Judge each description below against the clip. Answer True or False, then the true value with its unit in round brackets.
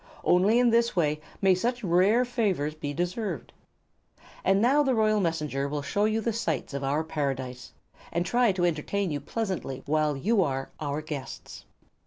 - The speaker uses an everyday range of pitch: False (6.7 semitones)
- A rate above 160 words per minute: True (170 wpm)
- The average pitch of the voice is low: False (175 Hz)